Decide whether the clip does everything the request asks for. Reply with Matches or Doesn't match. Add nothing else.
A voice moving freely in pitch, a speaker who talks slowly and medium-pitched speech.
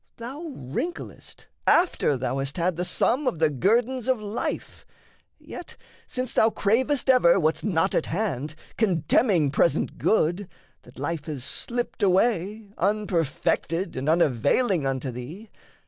Matches